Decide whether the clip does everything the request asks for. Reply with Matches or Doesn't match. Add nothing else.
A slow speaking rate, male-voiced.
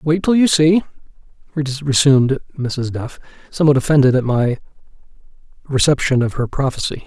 Matches